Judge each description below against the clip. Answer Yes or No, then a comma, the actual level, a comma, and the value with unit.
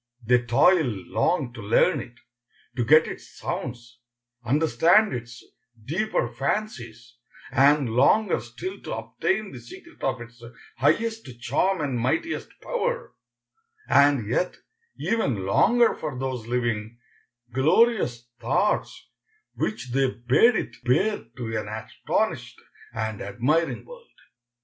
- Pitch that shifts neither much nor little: No, wide, 8.2 semitones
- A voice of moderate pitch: No, low, 130 Hz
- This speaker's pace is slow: Yes, slow, 115 wpm